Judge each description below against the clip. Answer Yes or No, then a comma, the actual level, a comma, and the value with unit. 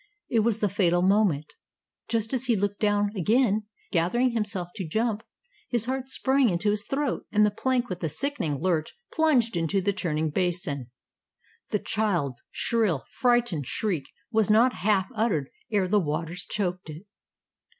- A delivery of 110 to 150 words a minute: No, average, 160 wpm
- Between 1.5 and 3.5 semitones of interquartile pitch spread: No, average, 4.7 semitones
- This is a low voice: No, high, 205 Hz